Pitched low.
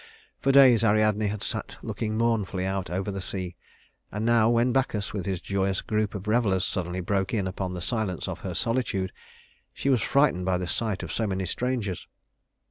Yes: low, 105 Hz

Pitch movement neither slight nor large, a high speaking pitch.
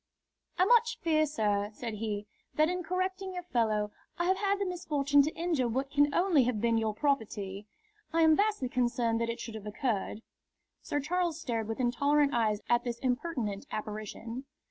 No: wide, 6.9 semitones; very high, 255 Hz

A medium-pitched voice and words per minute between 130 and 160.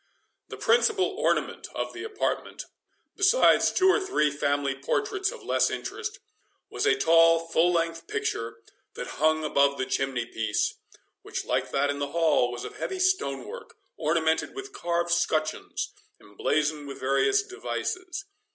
Yes: medium, 165 Hz; average, 150 wpm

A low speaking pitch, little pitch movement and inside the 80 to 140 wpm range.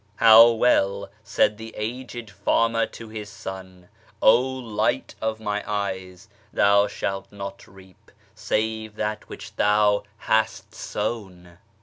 Yes: low, 105 Hz; narrow, 2.2 semitones; slow, 135 wpm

